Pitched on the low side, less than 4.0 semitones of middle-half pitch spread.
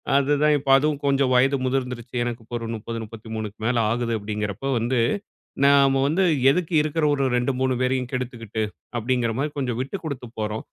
Yes: low, 125 Hz; average, 3.1 semitones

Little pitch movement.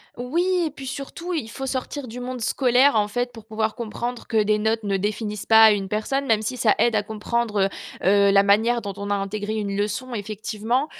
No: average, 3.0 semitones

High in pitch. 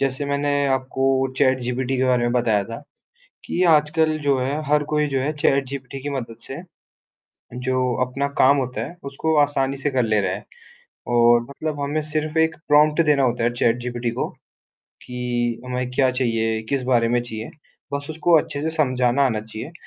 No: low, 130 Hz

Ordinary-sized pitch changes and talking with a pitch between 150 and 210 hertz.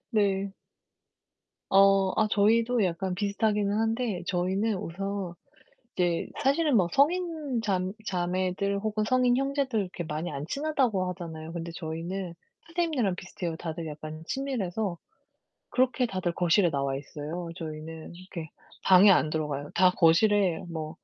Yes: average, 4.6 semitones; high, 190 Hz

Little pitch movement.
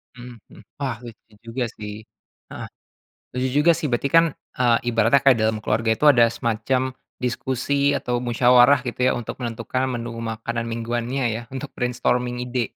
Yes: narrow, 1.9 semitones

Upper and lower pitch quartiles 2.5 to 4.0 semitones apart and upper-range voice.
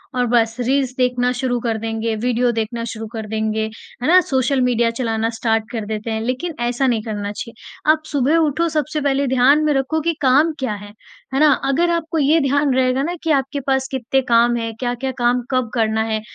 Yes: average, 3.5 semitones; very high, 250 Hz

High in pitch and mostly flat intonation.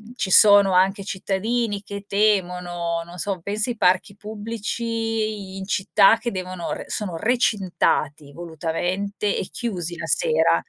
No: high, 200 Hz; average, 3.1 semitones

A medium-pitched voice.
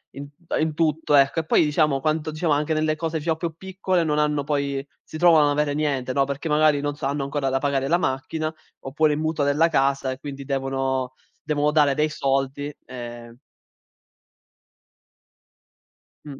Yes: medium, 145 Hz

